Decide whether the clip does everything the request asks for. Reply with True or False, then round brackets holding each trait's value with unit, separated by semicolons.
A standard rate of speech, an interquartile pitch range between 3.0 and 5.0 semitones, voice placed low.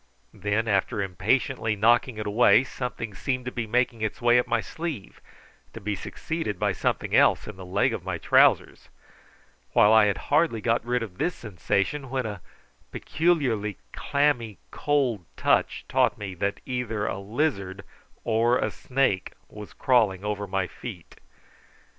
True (155 wpm; 3.7 semitones; 110 Hz)